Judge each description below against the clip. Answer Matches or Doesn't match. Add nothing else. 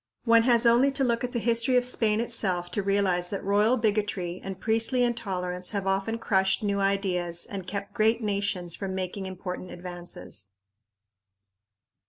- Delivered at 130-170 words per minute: Matches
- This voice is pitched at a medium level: Doesn't match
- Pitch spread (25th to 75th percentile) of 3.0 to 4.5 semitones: Matches